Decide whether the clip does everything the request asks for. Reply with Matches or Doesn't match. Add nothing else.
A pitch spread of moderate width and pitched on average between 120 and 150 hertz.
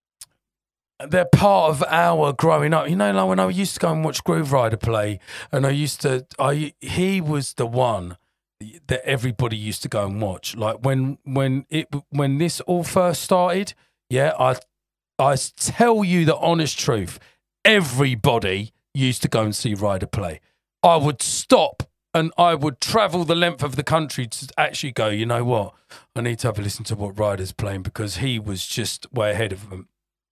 Doesn't match